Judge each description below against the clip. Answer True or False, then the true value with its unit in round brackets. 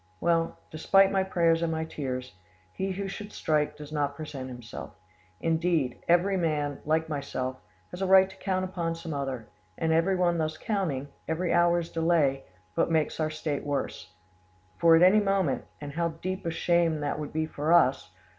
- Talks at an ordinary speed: True (175 wpm)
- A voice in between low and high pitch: True (160 Hz)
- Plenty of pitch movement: False (3.1 semitones)